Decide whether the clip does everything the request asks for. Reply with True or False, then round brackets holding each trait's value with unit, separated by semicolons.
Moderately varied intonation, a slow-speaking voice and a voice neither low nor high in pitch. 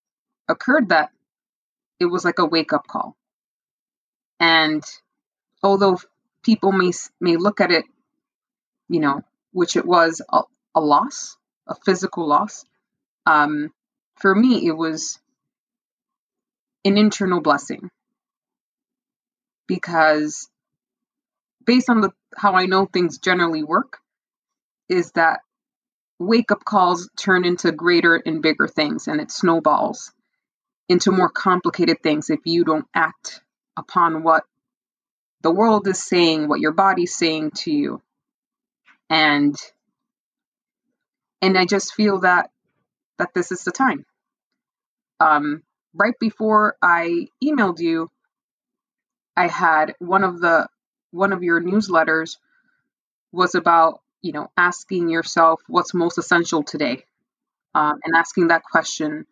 True (5.0 semitones; 120 wpm; 180 Hz)